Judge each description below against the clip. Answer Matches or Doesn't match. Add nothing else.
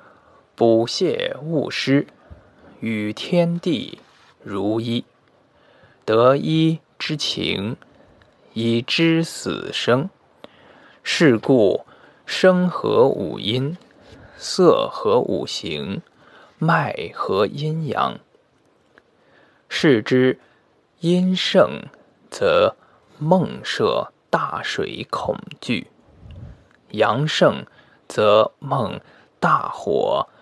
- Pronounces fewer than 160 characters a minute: Matches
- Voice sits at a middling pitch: Matches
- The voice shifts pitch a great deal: Matches